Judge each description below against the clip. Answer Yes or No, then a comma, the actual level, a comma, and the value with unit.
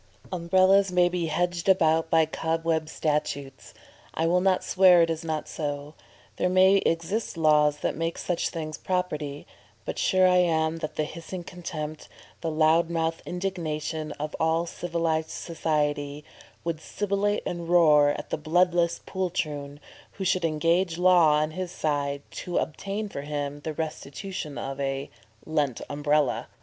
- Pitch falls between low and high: Yes, medium, 165 Hz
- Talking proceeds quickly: No, average, 150 wpm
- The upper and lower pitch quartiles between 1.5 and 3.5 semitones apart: Yes, average, 2.8 semitones